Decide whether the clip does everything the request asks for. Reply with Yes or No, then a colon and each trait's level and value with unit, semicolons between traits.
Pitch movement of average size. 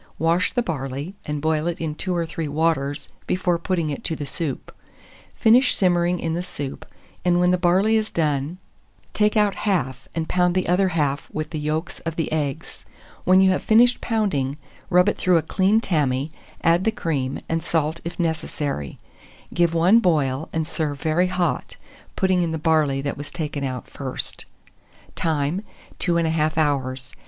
Yes: average, 3.4 semitones